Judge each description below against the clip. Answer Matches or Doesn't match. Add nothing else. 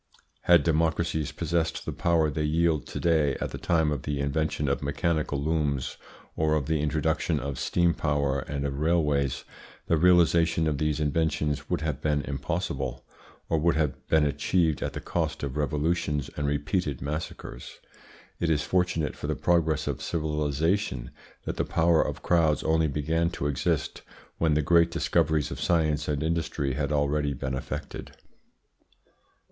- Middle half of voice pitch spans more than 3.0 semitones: Doesn't match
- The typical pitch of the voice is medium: Doesn't match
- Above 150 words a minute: Matches